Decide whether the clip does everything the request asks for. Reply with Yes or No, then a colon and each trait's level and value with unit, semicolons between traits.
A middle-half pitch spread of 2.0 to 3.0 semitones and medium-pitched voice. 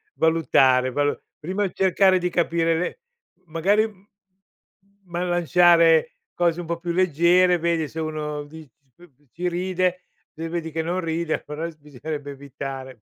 Yes: narrow, 2.6 semitones; medium, 165 Hz